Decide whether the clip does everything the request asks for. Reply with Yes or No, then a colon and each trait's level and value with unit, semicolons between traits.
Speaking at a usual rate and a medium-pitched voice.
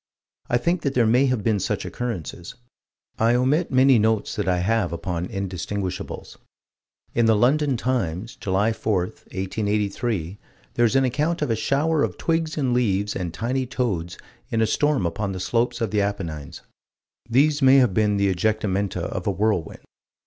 No: average, 170 wpm; low, 110 Hz